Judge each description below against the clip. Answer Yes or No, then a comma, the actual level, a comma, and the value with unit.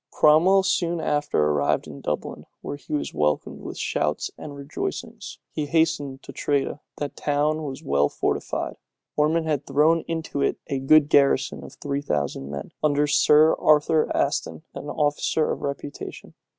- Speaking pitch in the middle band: Yes, medium, 145 Hz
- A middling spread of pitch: No, narrow, 2.1 semitones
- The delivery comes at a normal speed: Yes, average, 155 wpm